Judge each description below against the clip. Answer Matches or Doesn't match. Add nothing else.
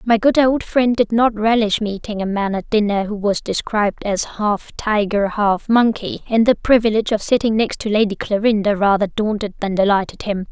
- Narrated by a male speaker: Doesn't match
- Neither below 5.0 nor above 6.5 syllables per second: Matches